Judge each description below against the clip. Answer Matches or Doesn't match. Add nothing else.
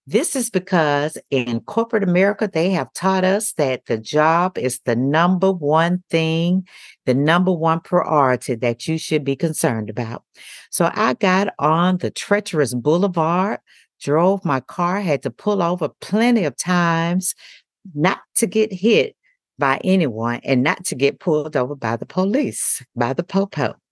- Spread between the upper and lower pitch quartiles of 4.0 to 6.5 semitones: Matches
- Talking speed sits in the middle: Matches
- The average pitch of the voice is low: Doesn't match